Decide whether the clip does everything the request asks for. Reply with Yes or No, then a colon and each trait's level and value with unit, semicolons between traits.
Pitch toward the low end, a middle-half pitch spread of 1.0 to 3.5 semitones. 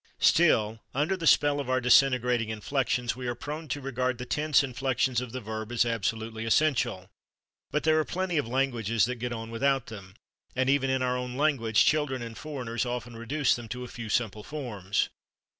Yes: low, 125 Hz; average, 3.2 semitones